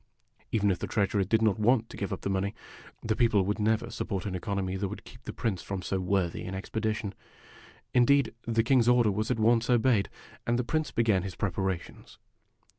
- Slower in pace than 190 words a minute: No, fast, 205 wpm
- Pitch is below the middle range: Yes, low, 105 Hz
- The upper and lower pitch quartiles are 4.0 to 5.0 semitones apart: No, average, 3.1 semitones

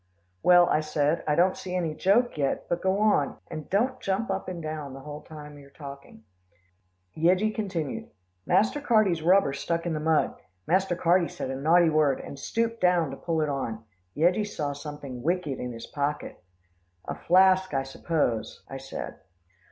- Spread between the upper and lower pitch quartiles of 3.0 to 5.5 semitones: Yes, average, 4.5 semitones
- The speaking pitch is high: No, medium, 160 Hz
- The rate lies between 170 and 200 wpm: Yes, average, 175 wpm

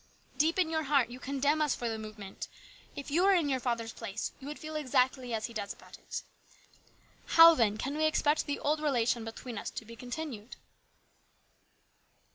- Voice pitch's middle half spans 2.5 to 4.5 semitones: No, average, 4.9 semitones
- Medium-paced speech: Yes, average, 190 wpm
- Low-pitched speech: No, very high, 265 Hz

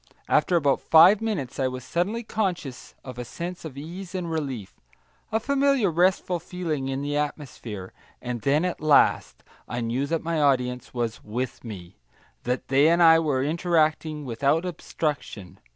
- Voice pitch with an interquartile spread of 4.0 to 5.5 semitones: Yes, average, 5.2 semitones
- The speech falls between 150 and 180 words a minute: Yes, average, 160 wpm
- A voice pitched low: No, medium, 150 Hz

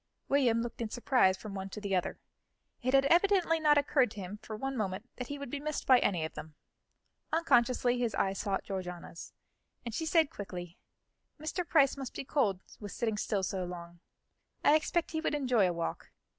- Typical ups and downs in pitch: No, wide, 6.7 semitones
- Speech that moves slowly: No, average, 200 wpm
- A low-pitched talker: No, high, 235 Hz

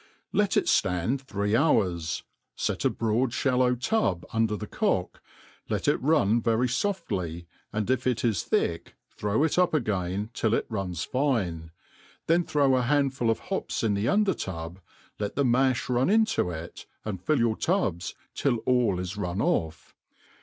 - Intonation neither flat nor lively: No, wide, 6.0 semitones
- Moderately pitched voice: No, low, 115 Hz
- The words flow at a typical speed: Yes, average, 165 wpm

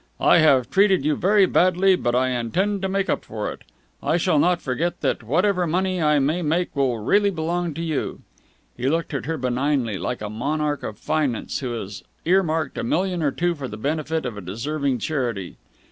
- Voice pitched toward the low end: No, medium, 155 Hz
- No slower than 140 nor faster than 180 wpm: No, average, 200 wpm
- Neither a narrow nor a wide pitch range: No, wide, 5.8 semitones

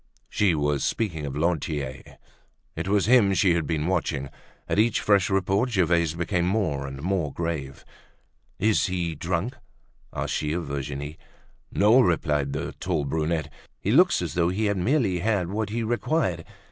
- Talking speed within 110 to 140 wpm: No, average, 165 wpm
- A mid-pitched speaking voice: No, very low, 85 Hz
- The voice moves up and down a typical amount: Yes, average, 5.0 semitones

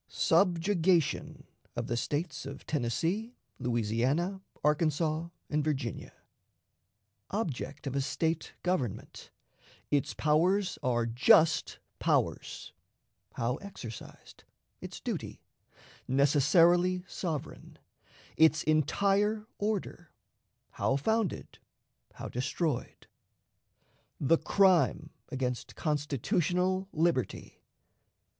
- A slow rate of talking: Yes, slow, 80 wpm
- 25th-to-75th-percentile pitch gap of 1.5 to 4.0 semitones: No, average, 4.9 semitones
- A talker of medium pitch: Yes, medium, 155 Hz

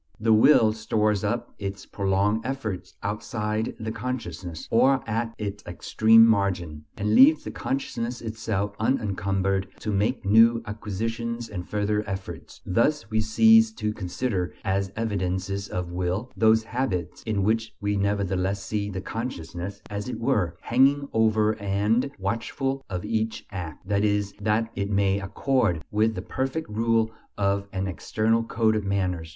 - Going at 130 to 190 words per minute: Yes, average, 145 wpm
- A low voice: Yes, low, 105 Hz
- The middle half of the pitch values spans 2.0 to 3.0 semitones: Yes, average, 2.7 semitones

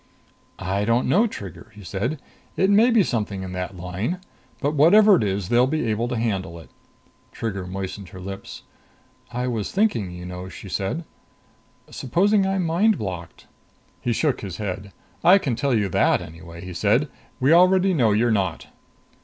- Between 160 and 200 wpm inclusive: Yes, average, 170 wpm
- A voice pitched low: Yes, low, 110 Hz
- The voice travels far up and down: Yes, wide, 8.8 semitones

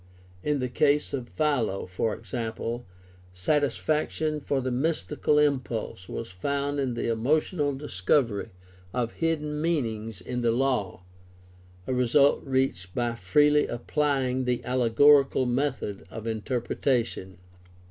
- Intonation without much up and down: No, average, 4.2 semitones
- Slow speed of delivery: Yes, slow, 120 wpm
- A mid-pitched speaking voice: No, low, 125 Hz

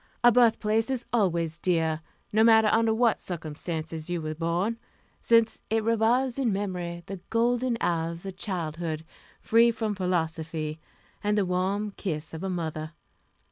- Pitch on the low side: No, medium, 185 Hz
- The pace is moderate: Yes, average, 145 wpm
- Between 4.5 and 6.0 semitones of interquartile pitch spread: Yes, average, 5.3 semitones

